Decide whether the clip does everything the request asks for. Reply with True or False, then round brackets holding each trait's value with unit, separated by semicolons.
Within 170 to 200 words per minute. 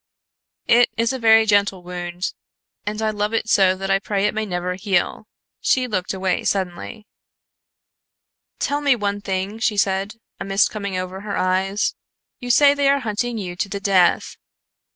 True (175 wpm)